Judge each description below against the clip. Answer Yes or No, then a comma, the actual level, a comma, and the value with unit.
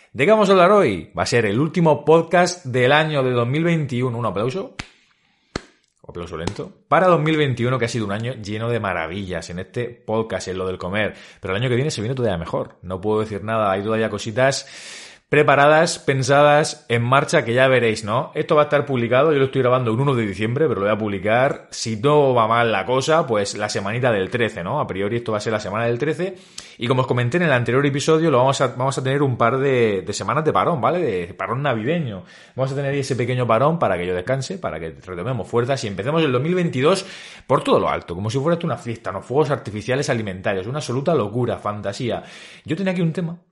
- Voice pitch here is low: Yes, low, 125 Hz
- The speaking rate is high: Yes, fast, 230 wpm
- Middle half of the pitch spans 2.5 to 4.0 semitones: No, average, 5.1 semitones